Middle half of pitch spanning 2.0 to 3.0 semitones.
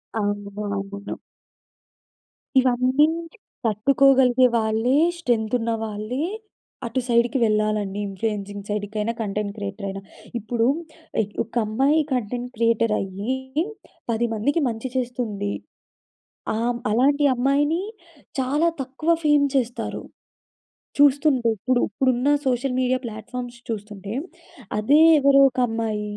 No: average, 3.6 semitones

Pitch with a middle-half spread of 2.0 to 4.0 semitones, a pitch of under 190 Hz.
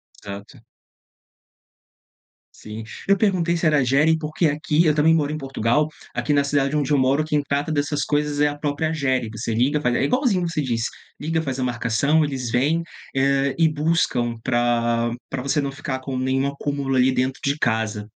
Yes: average, 3.0 semitones; medium, 140 Hz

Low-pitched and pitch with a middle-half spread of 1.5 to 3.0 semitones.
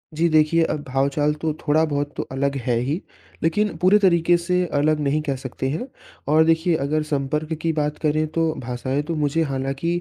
No: medium, 150 Hz; narrow, 2.6 semitones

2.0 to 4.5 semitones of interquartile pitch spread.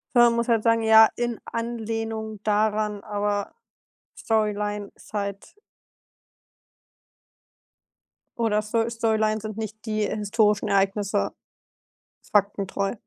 No: narrow, 1.4 semitones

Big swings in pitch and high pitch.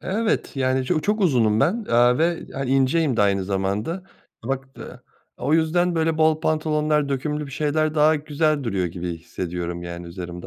No: wide, 7.5 semitones; medium, 140 Hz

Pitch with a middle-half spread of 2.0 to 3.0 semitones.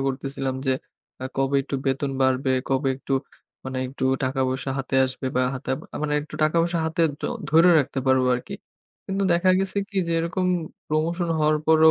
No: average, 3.8 semitones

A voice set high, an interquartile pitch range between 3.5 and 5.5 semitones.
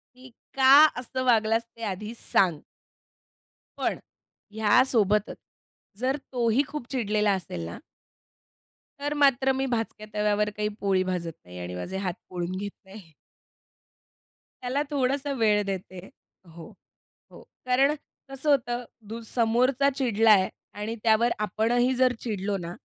Yes: high, 220 Hz; average, 4.4 semitones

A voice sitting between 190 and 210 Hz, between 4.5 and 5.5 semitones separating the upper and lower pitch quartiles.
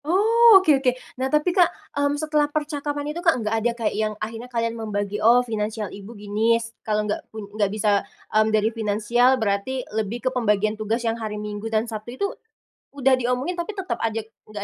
No: high, 230 Hz; average, 4.9 semitones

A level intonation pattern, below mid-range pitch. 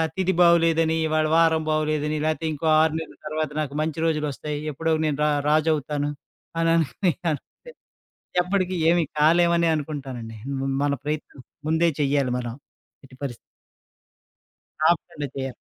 No: narrow, 2.3 semitones; medium, 155 Hz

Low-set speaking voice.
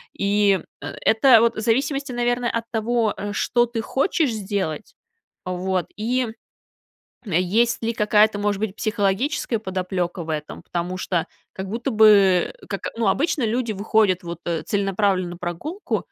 No: high, 210 Hz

